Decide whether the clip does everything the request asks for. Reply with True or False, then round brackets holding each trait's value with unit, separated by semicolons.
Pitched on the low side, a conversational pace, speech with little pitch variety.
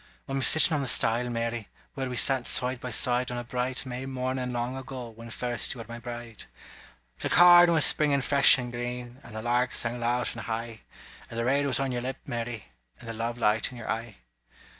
False (125 Hz; 220 wpm; 1.9 semitones)